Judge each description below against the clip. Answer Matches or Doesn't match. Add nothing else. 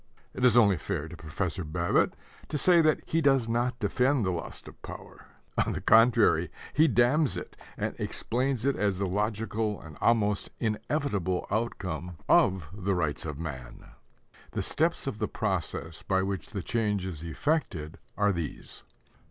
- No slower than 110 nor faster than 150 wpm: Doesn't match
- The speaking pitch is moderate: Doesn't match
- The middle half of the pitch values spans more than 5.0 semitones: Matches